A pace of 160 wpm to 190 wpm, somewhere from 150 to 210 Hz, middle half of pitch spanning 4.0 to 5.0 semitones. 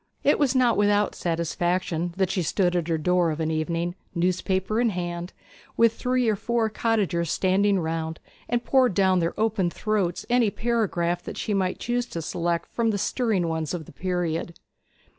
Yes: average, 180 wpm; medium, 185 Hz; average, 4.4 semitones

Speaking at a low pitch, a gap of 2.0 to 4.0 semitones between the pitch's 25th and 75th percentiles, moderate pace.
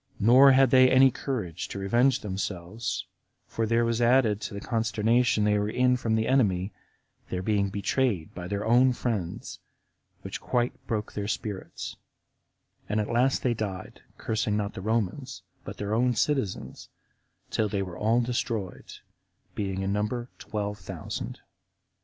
Yes: low, 110 Hz; average, 3.3 semitones; average, 150 wpm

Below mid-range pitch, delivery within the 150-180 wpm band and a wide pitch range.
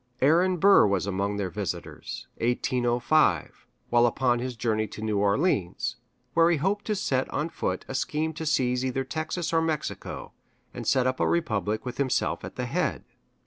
Yes: low, 130 Hz; average, 175 wpm; wide, 6.5 semitones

